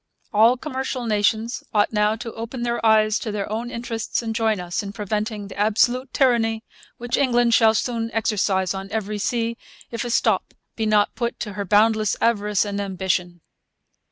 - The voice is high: Yes, high, 220 Hz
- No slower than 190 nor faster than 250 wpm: No, average, 175 wpm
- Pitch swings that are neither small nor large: No, narrow, 2.2 semitones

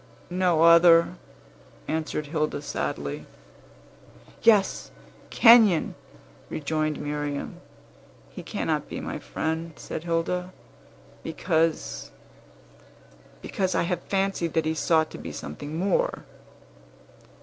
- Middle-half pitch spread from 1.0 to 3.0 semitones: Yes, narrow, 2.6 semitones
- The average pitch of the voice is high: No, medium, 165 Hz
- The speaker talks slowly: Yes, slow, 95 wpm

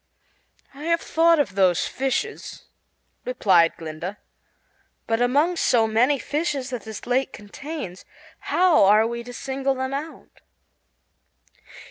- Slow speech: Yes, slow, 120 wpm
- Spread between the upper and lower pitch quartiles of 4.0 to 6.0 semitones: Yes, average, 5.1 semitones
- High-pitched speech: Yes, very high, 255 Hz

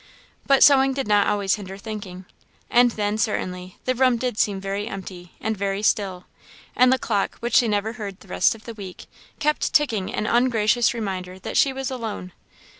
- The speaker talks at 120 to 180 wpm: No, average, 190 wpm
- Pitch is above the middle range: Yes, high, 215 Hz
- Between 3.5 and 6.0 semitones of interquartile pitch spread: Yes, average, 3.8 semitones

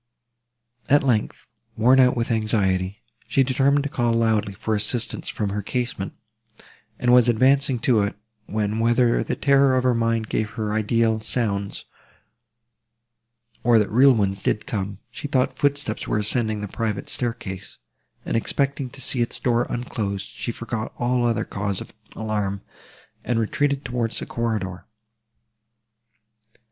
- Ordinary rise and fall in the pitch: Yes, average, 3.0 semitones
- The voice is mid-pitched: No, low, 115 Hz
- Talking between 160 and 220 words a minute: No, average, 145 wpm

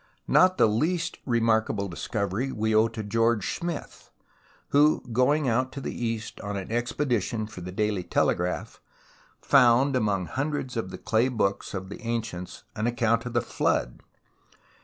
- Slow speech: No, average, 155 wpm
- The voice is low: Yes, low, 115 Hz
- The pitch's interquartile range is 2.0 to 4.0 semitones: Yes, average, 3.7 semitones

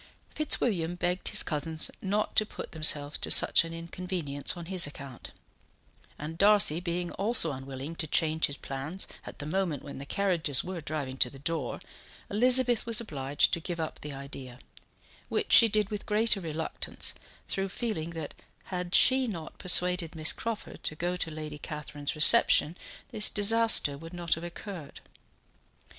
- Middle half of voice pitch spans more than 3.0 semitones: Yes, average, 4.5 semitones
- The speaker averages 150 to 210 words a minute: Yes, average, 160 wpm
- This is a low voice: No, medium, 165 Hz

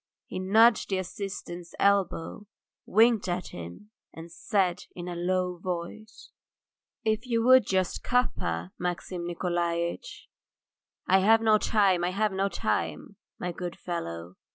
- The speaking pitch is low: No, medium, 185 Hz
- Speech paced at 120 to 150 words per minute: Yes, slow, 135 wpm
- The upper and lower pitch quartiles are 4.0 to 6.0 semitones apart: No, average, 3.5 semitones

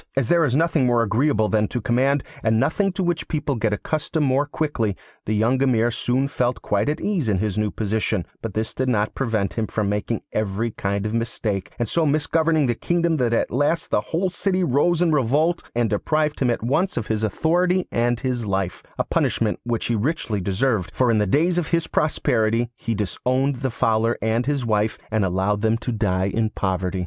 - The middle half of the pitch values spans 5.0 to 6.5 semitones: Yes, wide, 5.5 semitones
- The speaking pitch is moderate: No, low, 120 Hz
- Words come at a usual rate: No, fast, 210 wpm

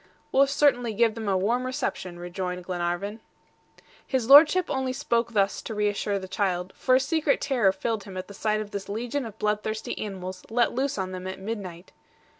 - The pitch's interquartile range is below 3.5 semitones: No, average, 4.5 semitones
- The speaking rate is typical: Yes, average, 190 wpm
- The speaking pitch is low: No, high, 210 Hz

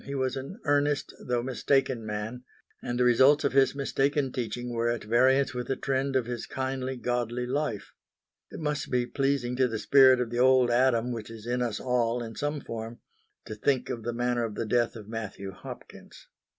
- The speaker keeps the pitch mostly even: Yes, narrow, 2.2 semitones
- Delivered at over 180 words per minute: Yes, average, 200 wpm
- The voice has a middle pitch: No, low, 125 Hz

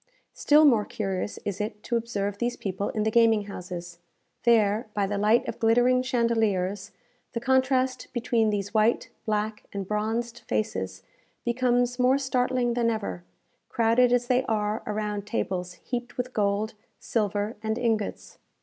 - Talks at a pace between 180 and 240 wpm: No, average, 150 wpm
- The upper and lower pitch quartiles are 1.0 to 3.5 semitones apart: Yes, average, 3.0 semitones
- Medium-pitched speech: No, high, 220 Hz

